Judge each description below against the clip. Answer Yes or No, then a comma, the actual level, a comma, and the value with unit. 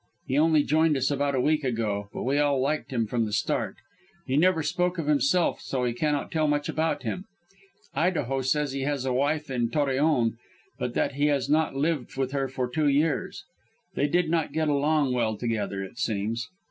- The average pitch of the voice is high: No, medium, 140 Hz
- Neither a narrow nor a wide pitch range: Yes, average, 3.5 semitones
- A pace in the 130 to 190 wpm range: No, average, 200 wpm